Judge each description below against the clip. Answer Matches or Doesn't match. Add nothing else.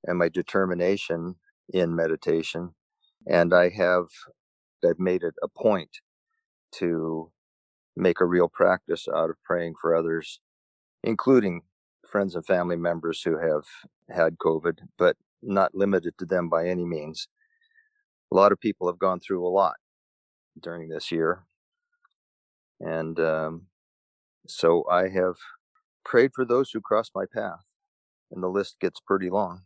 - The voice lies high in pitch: Doesn't match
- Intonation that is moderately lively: Matches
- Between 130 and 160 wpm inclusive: Matches